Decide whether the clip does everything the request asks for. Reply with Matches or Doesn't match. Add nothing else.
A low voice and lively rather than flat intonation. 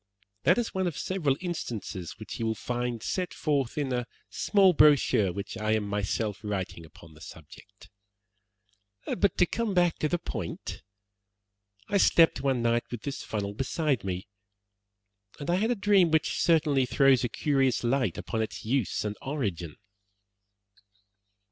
Matches